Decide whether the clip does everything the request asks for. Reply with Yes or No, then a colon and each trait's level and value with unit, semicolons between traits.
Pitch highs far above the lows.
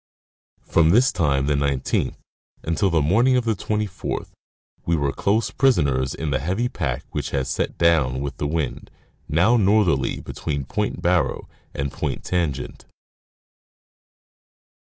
Yes: wide, 6.6 semitones